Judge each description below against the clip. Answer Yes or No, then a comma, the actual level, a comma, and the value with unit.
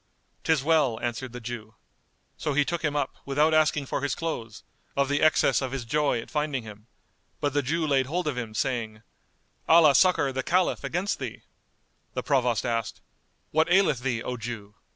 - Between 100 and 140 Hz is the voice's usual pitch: Yes, low, 135 Hz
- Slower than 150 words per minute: No, average, 185 wpm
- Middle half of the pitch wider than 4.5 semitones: No, average, 4.2 semitones